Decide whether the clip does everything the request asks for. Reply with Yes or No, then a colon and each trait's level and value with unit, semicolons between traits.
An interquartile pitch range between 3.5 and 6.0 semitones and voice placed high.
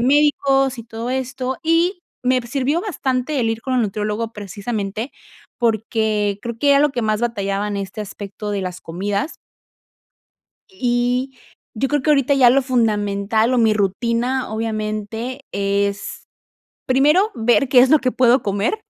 Yes: average, 4.0 semitones; high, 235 Hz